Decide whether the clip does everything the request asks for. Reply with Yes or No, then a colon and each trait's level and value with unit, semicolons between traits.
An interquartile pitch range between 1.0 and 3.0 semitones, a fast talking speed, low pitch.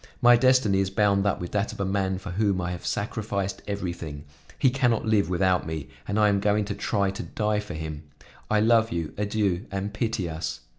Yes: average, 2.7 semitones; fast, 215 wpm; low, 100 Hz